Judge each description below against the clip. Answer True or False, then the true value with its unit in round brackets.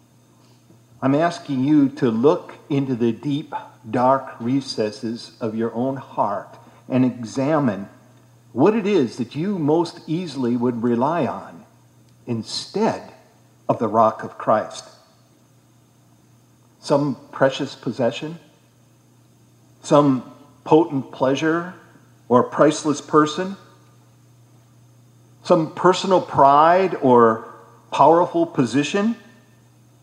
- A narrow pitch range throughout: False (4.4 semitones)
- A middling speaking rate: False (95 wpm)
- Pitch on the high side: False (130 Hz)